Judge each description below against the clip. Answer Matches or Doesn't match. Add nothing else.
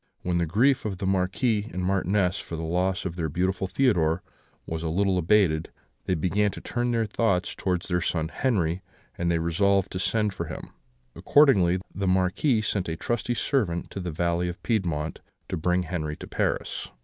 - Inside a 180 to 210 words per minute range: Matches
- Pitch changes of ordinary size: Matches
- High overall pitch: Doesn't match